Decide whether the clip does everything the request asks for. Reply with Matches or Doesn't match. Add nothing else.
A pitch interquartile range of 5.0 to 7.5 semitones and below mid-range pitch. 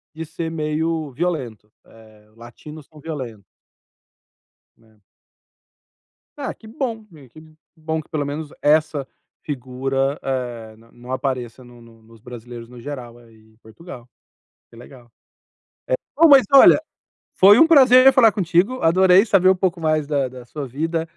Doesn't match